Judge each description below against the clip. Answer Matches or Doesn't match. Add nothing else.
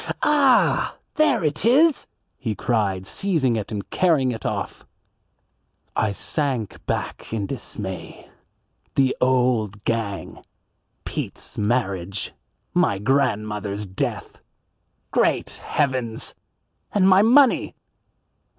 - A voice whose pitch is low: Matches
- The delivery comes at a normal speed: Doesn't match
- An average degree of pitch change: Doesn't match